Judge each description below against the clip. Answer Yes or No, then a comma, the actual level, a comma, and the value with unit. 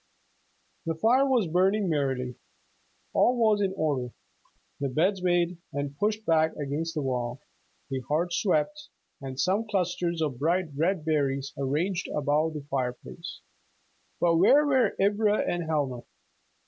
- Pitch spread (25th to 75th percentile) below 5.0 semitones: No, wide, 5.5 semitones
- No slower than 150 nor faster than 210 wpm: No, slow, 135 wpm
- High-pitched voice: No, medium, 160 Hz